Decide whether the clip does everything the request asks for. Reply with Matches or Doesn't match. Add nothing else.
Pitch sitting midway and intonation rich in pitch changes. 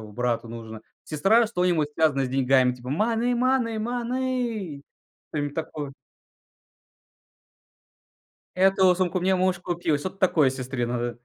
Matches